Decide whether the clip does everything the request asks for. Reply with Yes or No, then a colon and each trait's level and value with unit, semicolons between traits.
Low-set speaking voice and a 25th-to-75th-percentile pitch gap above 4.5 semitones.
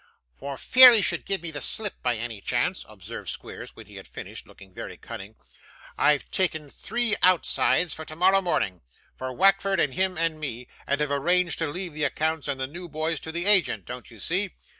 No: medium, 160 Hz; average, 5.0 semitones